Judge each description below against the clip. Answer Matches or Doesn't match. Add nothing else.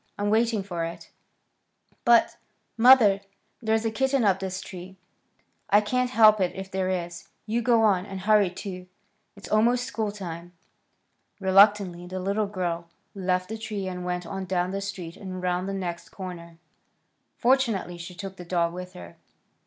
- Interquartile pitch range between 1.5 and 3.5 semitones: Matches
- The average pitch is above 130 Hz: Matches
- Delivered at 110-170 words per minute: Matches